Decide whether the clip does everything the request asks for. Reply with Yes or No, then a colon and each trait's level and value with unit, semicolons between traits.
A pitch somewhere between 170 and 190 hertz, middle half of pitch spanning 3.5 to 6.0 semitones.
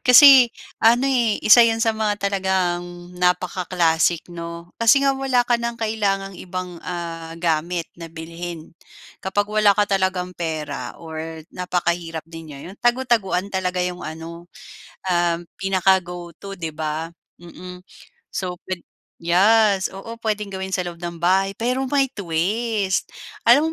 Yes: medium, 185 Hz; average, 3.8 semitones